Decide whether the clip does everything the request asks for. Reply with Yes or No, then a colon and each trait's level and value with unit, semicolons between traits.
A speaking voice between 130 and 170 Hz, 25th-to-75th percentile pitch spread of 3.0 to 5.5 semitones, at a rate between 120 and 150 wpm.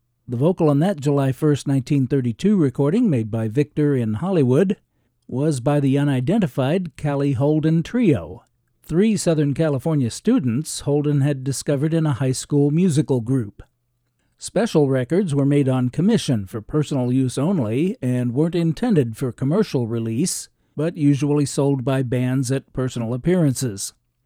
Yes: medium, 140 Hz; average, 3.6 semitones; average, 140 wpm